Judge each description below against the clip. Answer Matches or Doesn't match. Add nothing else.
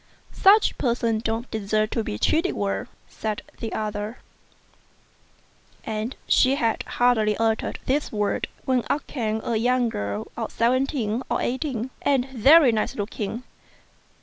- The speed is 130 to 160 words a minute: Matches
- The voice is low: Doesn't match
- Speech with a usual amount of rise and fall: Matches